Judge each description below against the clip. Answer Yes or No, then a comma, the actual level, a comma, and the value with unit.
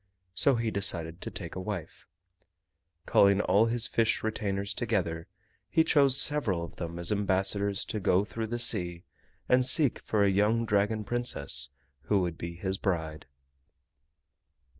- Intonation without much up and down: No, average, 4.4 semitones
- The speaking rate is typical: Yes, average, 150 wpm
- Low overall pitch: Yes, low, 100 Hz